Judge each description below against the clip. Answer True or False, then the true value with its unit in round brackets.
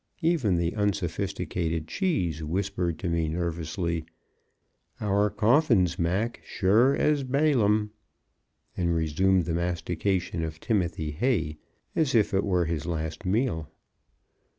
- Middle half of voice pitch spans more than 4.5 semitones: False (4.1 semitones)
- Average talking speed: False (115 wpm)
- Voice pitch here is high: False (90 Hz)